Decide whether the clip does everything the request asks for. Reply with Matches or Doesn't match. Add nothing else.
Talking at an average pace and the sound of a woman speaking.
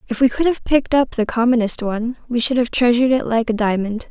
Doesn't match